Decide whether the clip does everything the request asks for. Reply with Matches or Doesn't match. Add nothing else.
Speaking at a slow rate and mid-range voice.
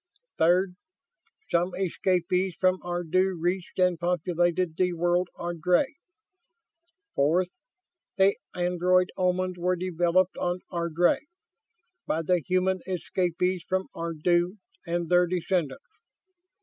Matches